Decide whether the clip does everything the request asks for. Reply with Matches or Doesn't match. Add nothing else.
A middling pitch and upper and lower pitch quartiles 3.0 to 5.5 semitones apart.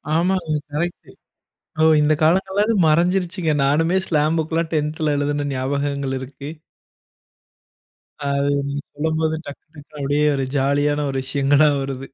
Doesn't match